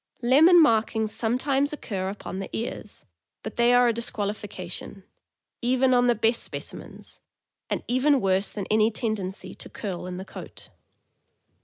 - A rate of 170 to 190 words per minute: No, average, 150 wpm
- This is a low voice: No, high, 225 Hz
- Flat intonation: No, average, 3.9 semitones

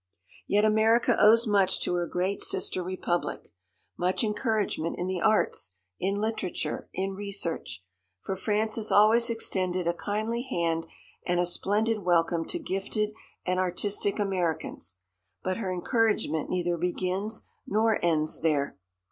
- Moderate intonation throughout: Yes, average, 3.5 semitones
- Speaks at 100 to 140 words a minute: Yes, slow, 135 wpm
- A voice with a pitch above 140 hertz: Yes, high, 190 Hz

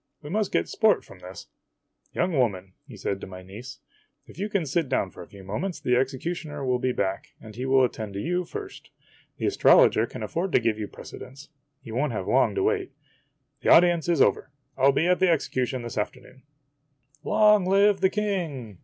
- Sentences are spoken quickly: Yes, fast, 215 wpm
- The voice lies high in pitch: No, low, 135 Hz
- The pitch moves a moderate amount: No, wide, 7.9 semitones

